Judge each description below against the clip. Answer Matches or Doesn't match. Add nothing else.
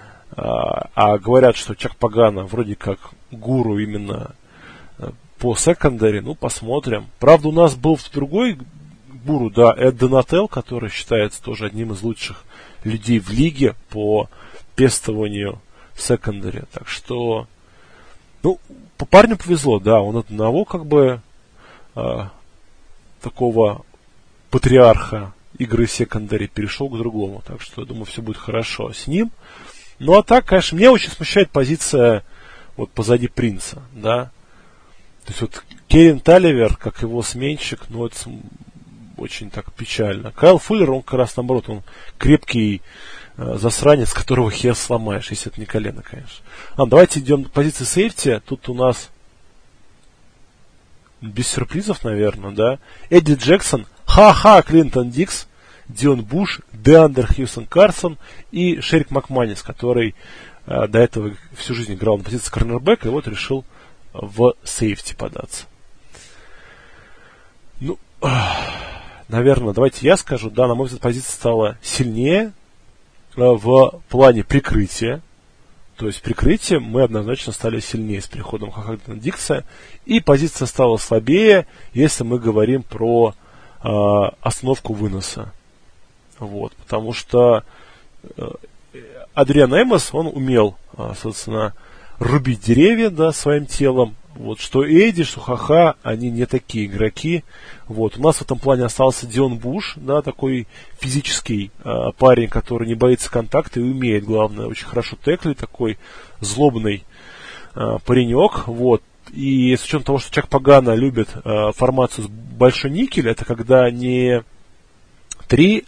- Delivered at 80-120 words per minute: Doesn't match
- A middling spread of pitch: Matches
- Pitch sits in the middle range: Doesn't match